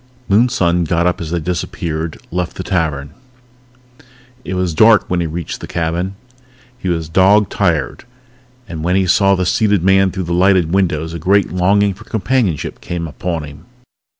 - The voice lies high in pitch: No, very low, 90 Hz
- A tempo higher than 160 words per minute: Yes, average, 170 wpm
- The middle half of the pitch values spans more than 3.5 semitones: No, average, 2.7 semitones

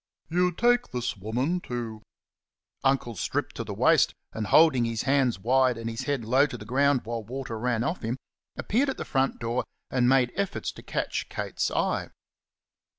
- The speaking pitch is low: Yes, low, 125 Hz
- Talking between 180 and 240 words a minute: Yes, average, 185 wpm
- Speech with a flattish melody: No, average, 3.5 semitones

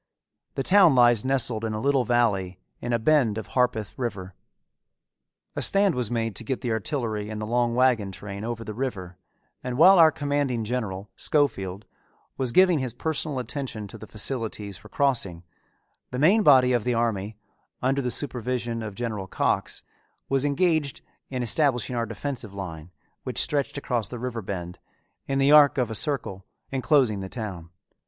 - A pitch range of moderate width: Yes, average, 4.2 semitones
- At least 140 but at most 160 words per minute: No, average, 170 wpm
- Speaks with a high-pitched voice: No, low, 120 Hz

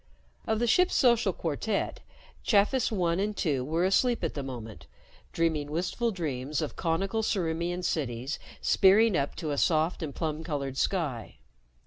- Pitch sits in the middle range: Yes, medium, 165 Hz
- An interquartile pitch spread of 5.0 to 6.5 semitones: Yes, average, 5.3 semitones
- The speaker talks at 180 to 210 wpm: No, average, 150 wpm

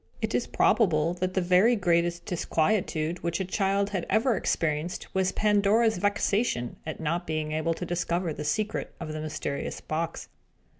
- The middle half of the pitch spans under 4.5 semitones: Yes, average, 4.1 semitones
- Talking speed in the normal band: Yes, average, 160 wpm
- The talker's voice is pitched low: No, medium, 175 Hz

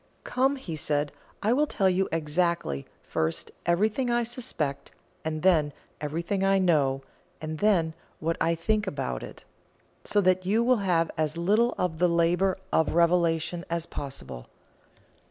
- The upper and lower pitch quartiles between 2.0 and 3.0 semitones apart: No, average, 3.8 semitones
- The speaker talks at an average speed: Yes, average, 150 wpm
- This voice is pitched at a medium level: Yes, medium, 170 Hz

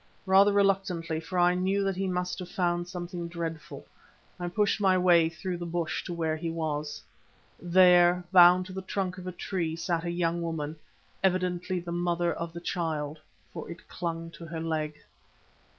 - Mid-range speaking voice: Yes, medium, 175 Hz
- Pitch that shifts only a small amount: Yes, narrow, 1.7 semitones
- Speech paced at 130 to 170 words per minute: No, average, 180 wpm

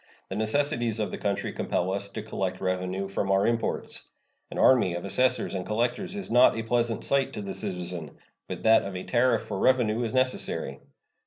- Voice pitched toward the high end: No, low, 110 Hz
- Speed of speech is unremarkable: Yes, average, 190 wpm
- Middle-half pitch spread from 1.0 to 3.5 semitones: No, average, 4.2 semitones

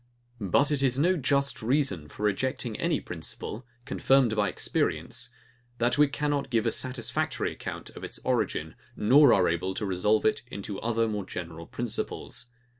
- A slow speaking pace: No, average, 160 wpm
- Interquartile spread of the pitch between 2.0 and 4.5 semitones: No, average, 5.0 semitones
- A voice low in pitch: Yes, low, 120 Hz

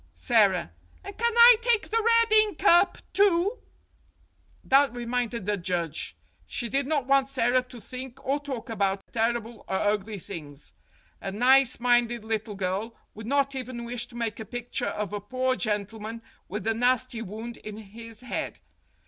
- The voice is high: Yes, high, 235 Hz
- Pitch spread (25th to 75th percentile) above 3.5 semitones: Yes, average, 3.9 semitones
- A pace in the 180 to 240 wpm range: No, average, 165 wpm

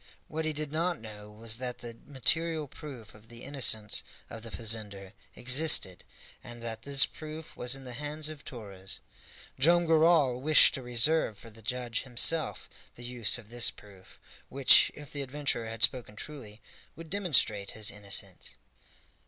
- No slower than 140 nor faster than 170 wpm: Yes, average, 160 wpm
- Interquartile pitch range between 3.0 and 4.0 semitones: No, average, 5.2 semitones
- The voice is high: No, low, 125 Hz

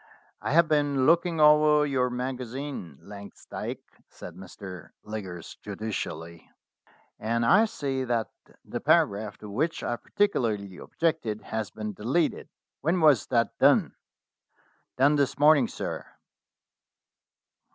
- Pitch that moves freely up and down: Yes, wide, 6.3 semitones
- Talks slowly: Yes, slow, 120 wpm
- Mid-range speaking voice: No, low, 125 Hz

